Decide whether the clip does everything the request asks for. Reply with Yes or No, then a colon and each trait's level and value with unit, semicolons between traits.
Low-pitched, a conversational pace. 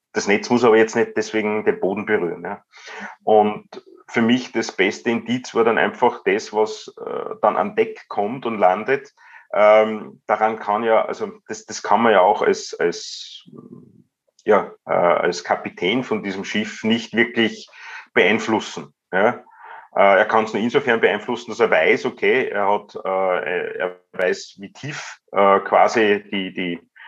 Yes: low, 115 Hz; average, 165 wpm